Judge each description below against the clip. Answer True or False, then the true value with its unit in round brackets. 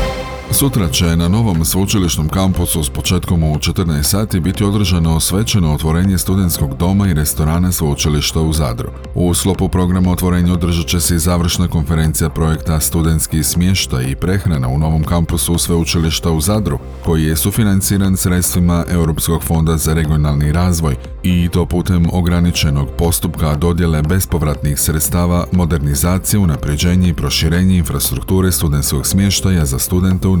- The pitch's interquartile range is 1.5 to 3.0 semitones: True (2.6 semitones)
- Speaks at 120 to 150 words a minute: True (140 wpm)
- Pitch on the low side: True (85 Hz)